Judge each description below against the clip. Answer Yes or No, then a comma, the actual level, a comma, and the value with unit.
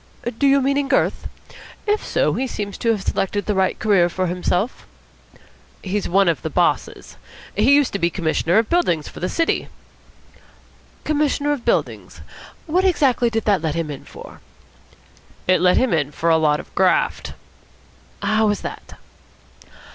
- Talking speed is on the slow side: No, average, 165 wpm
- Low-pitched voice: No, high, 205 Hz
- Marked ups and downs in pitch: Yes, wide, 7.4 semitones